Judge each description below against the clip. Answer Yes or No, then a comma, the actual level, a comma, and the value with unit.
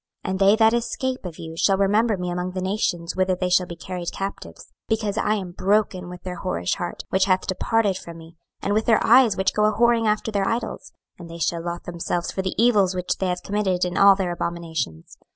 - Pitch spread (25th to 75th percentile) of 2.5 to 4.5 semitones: Yes, average, 3.2 semitones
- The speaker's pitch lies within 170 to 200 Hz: Yes, high, 190 Hz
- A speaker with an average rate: No, fast, 230 wpm